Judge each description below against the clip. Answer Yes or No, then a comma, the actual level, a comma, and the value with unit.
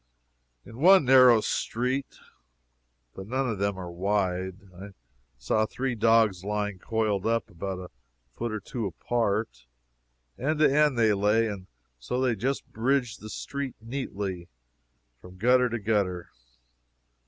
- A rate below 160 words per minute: Yes, average, 140 wpm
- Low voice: Yes, low, 110 Hz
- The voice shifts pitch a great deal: No, average, 4.2 semitones